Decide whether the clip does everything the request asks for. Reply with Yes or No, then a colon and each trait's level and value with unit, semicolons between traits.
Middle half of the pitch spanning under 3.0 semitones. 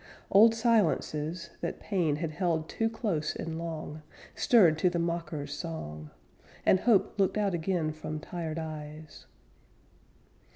No: average, 3.4 semitones